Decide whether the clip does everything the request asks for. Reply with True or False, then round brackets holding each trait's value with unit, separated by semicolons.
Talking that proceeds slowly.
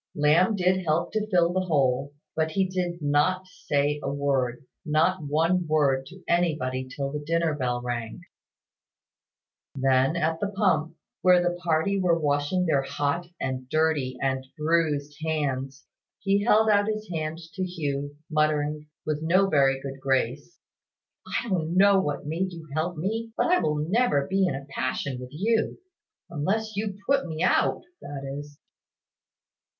False (155 wpm)